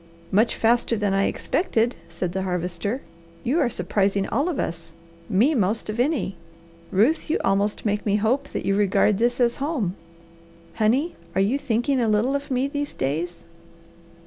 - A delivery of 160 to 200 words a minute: Yes, average, 170 wpm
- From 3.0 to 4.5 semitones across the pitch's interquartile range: No, average, 5.2 semitones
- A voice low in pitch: No, high, 220 Hz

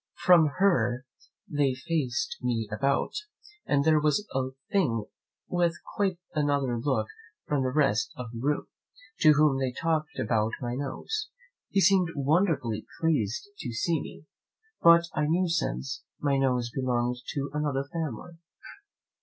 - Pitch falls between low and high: Yes, medium, 145 Hz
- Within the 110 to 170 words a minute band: Yes, average, 140 wpm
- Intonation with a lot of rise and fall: No, average, 4.6 semitones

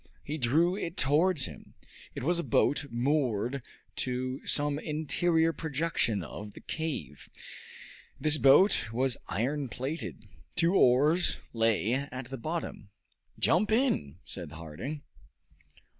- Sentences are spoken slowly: Yes, slow, 120 wpm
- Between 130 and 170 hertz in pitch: Yes, medium, 140 Hz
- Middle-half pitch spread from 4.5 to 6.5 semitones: Yes, average, 5.1 semitones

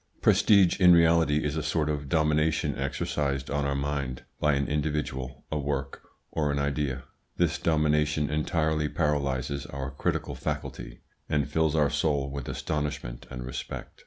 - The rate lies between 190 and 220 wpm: No, average, 150 wpm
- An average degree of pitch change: No, narrow, 1.8 semitones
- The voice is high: No, very low, 75 Hz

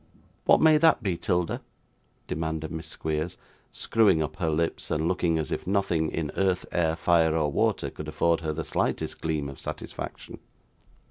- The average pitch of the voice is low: Yes, very low, 80 Hz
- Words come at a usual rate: Yes, average, 170 wpm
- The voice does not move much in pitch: Yes, narrow, 2.3 semitones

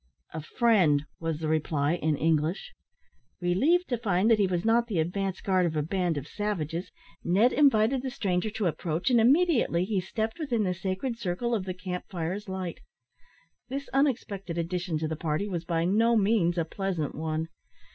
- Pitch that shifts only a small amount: No, average, 5.1 semitones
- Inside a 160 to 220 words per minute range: Yes, average, 180 wpm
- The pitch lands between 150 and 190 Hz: Yes, medium, 185 Hz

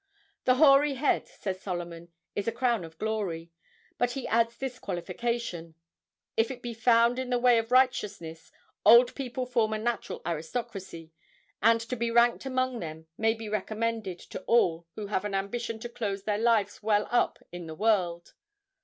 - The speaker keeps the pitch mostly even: No, average, 4.2 semitones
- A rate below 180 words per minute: Yes, average, 170 wpm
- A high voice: Yes, high, 225 Hz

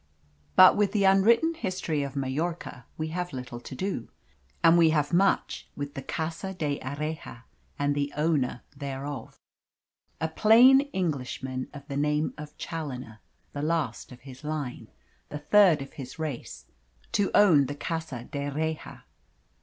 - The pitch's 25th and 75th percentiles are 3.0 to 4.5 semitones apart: Yes, average, 3.8 semitones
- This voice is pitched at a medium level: Yes, medium, 150 Hz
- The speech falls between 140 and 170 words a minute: Yes, average, 145 wpm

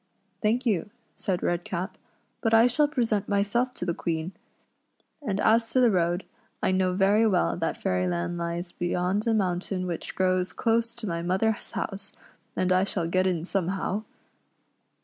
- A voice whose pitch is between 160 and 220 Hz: Yes, high, 190 Hz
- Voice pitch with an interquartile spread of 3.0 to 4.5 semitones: Yes, average, 3.9 semitones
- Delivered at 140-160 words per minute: No, average, 170 wpm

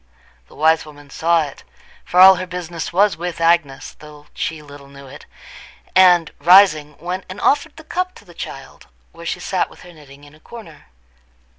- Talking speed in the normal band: Yes, average, 185 wpm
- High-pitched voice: No, medium, 165 Hz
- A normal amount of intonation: Yes, average, 3.7 semitones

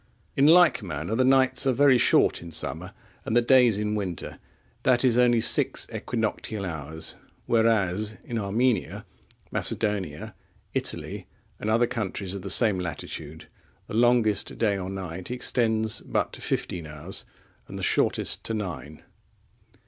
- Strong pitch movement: No, average, 4.8 semitones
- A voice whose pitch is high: No, low, 110 Hz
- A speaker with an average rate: Yes, average, 145 wpm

